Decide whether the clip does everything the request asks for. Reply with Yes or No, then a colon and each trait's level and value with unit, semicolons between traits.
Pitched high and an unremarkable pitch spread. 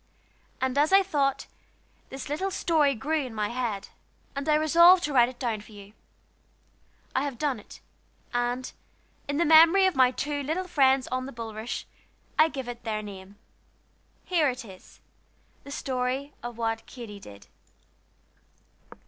Yes: very high, 260 Hz; average, 4.4 semitones